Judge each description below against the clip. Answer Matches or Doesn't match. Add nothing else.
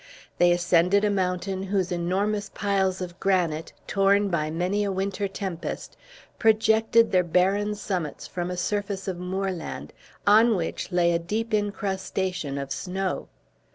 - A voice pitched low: Doesn't match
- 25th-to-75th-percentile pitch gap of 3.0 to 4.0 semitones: Doesn't match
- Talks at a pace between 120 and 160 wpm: Matches